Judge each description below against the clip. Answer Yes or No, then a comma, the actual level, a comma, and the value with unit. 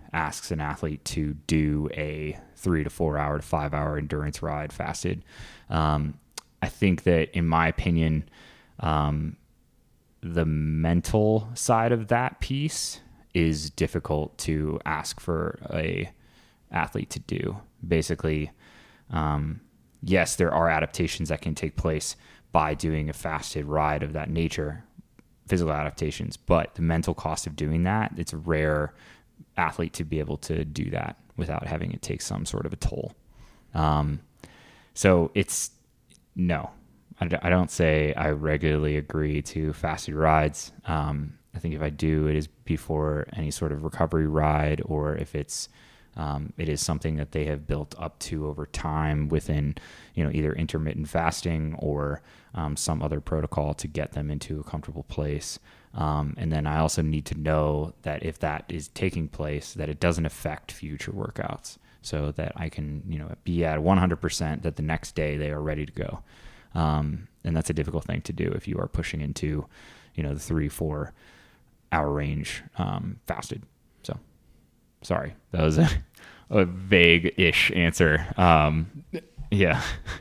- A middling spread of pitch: No, narrow, 1.7 semitones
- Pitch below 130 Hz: Yes, very low, 75 Hz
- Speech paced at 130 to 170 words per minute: Yes, average, 160 wpm